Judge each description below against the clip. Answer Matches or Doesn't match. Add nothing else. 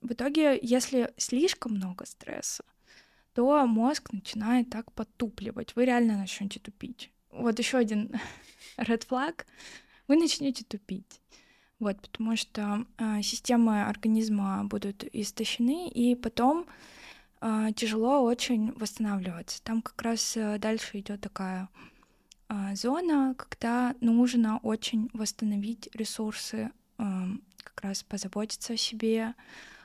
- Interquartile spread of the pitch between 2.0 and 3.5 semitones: Matches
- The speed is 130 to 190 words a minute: Doesn't match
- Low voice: Doesn't match